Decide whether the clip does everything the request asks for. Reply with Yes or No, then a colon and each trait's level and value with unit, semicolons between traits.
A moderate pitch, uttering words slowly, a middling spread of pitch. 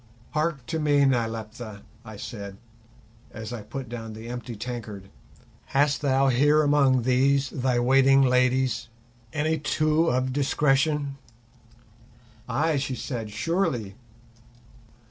No: low, 130 Hz; slow, 115 wpm; average, 3.5 semitones